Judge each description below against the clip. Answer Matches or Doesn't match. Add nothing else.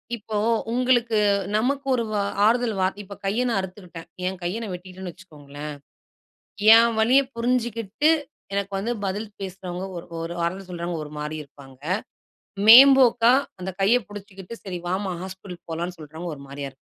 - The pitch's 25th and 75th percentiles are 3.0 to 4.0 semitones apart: Doesn't match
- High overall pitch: Matches